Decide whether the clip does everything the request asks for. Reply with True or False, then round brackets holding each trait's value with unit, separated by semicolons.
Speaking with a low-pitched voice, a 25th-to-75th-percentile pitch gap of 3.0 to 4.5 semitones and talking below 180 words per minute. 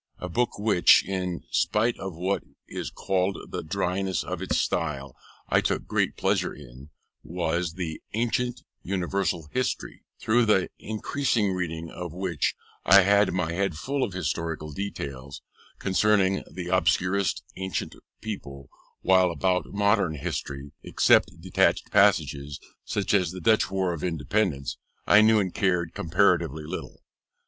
True (90 Hz; 3.4 semitones; 140 wpm)